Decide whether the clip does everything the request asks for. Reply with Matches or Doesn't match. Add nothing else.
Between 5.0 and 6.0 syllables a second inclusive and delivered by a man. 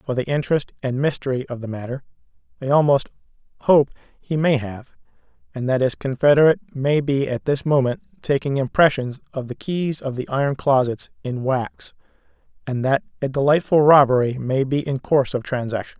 Matches